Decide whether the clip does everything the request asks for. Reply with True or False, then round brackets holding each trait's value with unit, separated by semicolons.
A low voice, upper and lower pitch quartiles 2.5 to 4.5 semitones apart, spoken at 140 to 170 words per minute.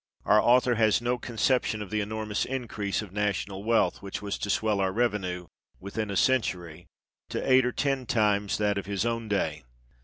False (105 Hz; 2.9 semitones; 185 wpm)